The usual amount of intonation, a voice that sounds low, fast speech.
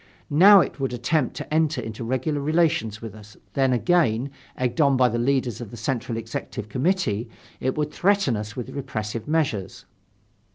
No: average, 5.0 semitones; low, 130 Hz; average, 170 wpm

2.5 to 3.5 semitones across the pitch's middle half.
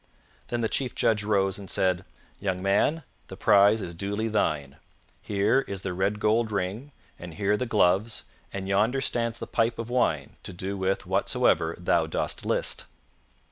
Yes: average, 3.0 semitones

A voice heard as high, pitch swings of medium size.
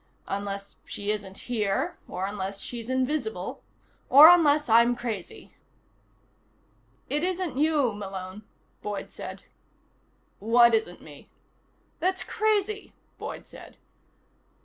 No: high, 230 Hz; wide, 7.0 semitones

